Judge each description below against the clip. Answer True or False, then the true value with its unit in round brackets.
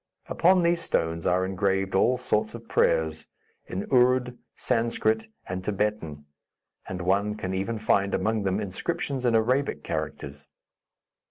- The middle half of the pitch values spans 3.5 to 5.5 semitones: True (4.9 semitones)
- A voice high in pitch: False (105 Hz)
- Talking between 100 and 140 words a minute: True (135 wpm)